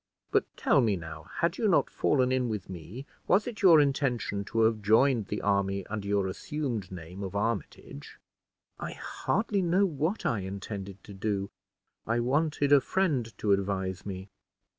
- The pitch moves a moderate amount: No, wide, 6.4 semitones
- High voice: No, low, 110 Hz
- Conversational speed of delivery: Yes, average, 165 wpm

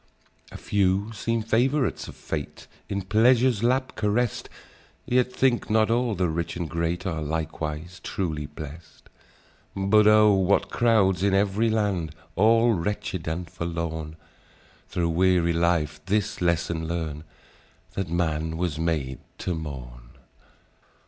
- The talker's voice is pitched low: Yes, very low, 90 Hz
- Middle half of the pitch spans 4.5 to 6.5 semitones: Yes, average, 4.9 semitones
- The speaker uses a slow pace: Yes, slow, 130 wpm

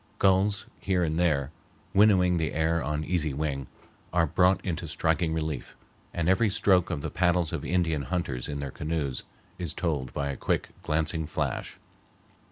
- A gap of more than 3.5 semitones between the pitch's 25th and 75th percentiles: No, average, 3.2 semitones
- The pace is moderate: Yes, average, 165 wpm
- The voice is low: Yes, very low, 80 Hz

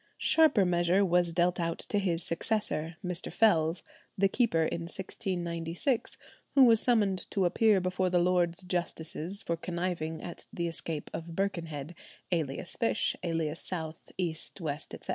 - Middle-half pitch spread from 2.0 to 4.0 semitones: Yes, narrow, 2.6 semitones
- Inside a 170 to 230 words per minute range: No, average, 145 wpm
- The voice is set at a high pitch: No, medium, 175 Hz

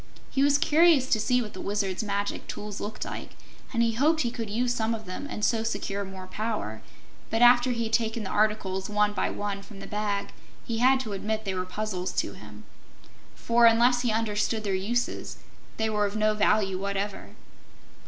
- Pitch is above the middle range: Yes, high, 215 Hz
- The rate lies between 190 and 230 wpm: Yes, average, 195 wpm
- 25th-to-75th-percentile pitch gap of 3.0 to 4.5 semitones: No, narrow, 2.6 semitones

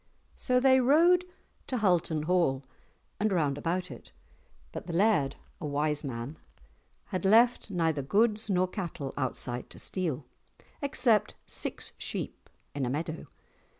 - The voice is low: No, medium, 175 Hz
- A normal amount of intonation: No, wide, 6.9 semitones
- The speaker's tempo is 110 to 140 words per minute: Yes, slow, 135 wpm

